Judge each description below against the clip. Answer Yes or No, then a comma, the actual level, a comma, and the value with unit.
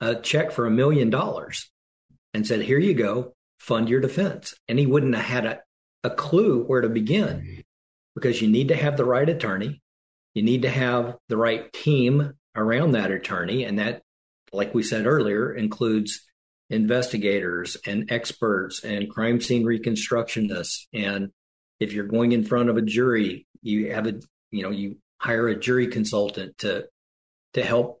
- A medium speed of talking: Yes, average, 170 wpm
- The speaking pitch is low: Yes, low, 115 Hz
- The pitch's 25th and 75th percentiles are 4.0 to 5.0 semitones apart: No, average, 2.8 semitones